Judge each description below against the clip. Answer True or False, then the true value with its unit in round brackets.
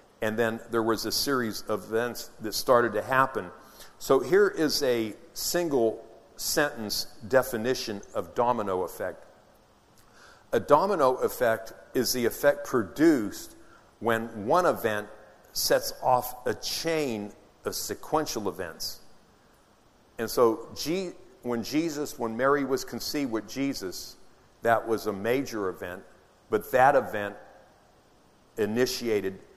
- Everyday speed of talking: False (120 wpm)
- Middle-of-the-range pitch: False (120 Hz)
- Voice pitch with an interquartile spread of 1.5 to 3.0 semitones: False (4.2 semitones)